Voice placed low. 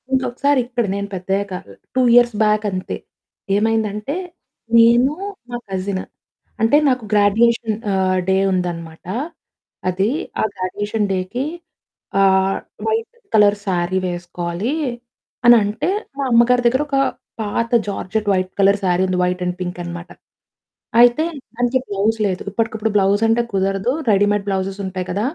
No: high, 205 Hz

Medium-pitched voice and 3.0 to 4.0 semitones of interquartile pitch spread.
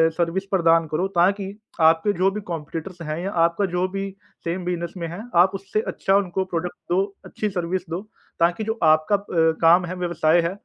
No: medium, 175 Hz; narrow, 2.4 semitones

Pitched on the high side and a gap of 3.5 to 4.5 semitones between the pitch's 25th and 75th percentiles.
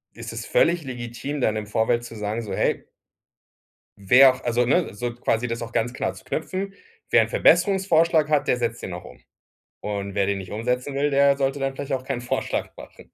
No: low, 125 Hz; average, 4.1 semitones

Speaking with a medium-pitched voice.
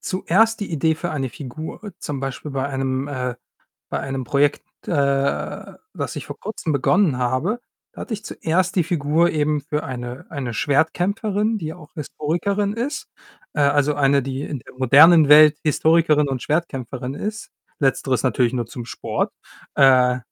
Yes: medium, 150 Hz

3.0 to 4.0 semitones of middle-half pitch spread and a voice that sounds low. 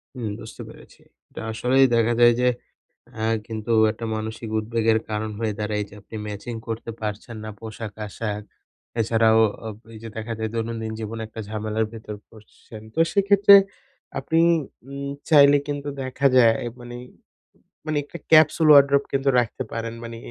Yes: average, 3.5 semitones; low, 115 Hz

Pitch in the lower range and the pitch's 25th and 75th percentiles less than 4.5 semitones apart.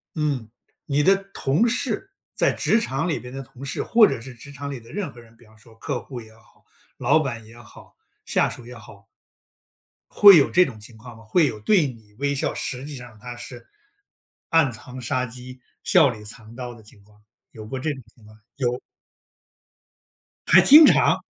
Yes: low, 125 Hz; average, 3.9 semitones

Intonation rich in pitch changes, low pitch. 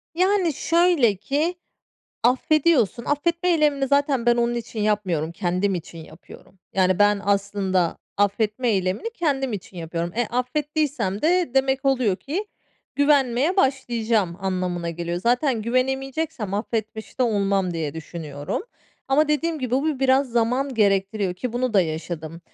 No: wide, 6.5 semitones; high, 235 Hz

